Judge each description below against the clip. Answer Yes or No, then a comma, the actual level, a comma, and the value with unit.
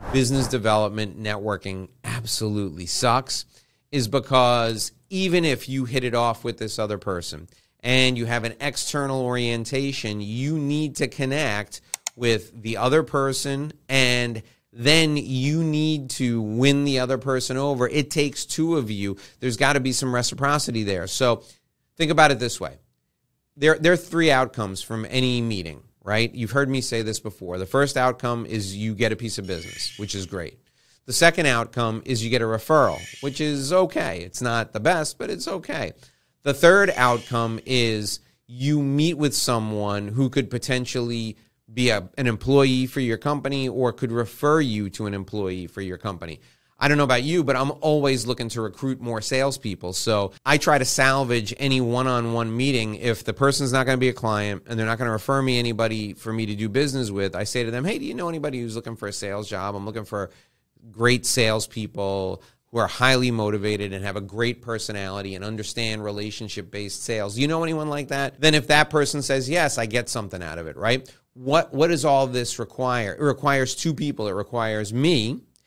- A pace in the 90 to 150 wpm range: No, average, 190 wpm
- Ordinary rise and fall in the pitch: Yes, average, 4.2 semitones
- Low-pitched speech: Yes, low, 120 Hz